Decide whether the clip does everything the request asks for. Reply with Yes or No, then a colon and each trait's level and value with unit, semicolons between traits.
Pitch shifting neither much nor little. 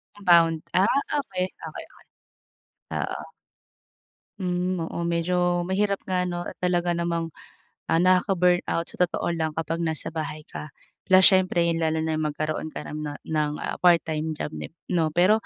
No: narrow, 2.2 semitones